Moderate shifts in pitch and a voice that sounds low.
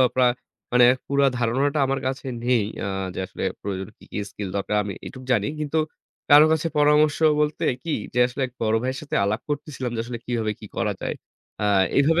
Yes: average, 4.2 semitones; low, 130 Hz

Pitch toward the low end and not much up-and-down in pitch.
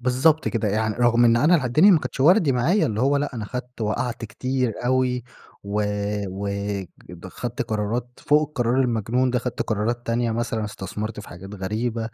No: low, 120 Hz; average, 3.0 semitones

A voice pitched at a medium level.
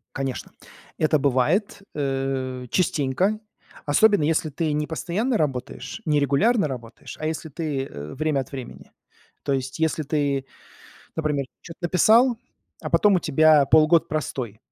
Yes: medium, 150 Hz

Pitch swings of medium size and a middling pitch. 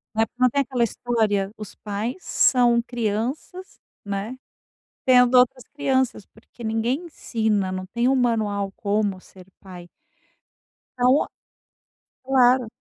No: average, 3.6 semitones; high, 235 Hz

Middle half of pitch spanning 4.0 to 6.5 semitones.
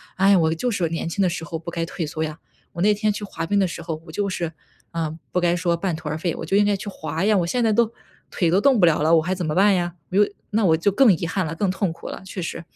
No: average, 3.4 semitones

